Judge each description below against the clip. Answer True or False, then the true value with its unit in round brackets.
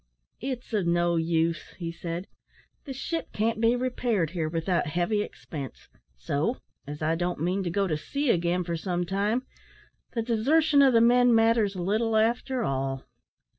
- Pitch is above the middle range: True (195 Hz)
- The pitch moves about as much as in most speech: False (5.7 semitones)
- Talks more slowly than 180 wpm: True (165 wpm)